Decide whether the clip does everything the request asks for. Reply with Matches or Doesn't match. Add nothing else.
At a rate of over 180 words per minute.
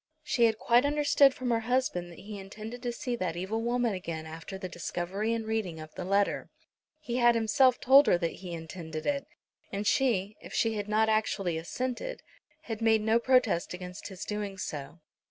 Matches